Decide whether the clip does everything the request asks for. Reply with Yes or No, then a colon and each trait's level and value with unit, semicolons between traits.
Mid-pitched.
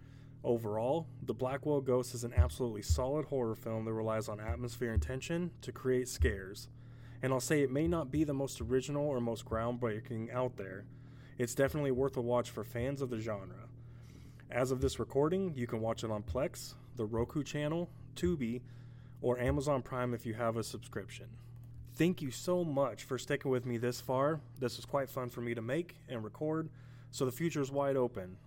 No: low, 125 Hz